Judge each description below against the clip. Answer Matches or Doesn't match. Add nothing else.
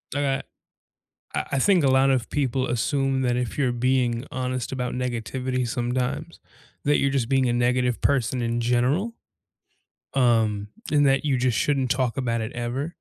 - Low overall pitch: Matches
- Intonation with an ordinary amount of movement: Doesn't match